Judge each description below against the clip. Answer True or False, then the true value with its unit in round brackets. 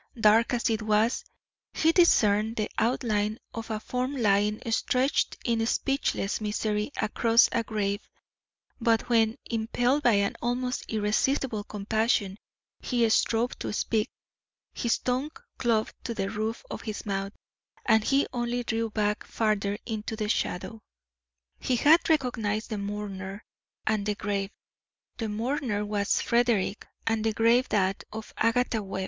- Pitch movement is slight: True (2.3 semitones)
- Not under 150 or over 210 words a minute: False (140 wpm)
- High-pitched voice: True (220 Hz)